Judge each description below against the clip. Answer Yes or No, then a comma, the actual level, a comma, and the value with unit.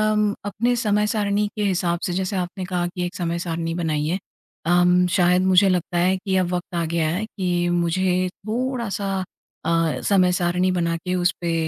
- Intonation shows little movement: Yes, narrow, 2.0 semitones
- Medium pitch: Yes, medium, 180 Hz